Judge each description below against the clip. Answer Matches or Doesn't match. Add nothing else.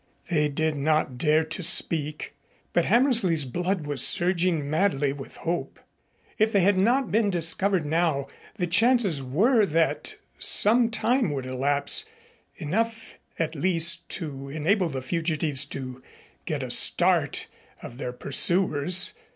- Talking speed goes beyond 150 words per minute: Doesn't match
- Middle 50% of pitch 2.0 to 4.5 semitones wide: Doesn't match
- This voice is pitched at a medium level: Matches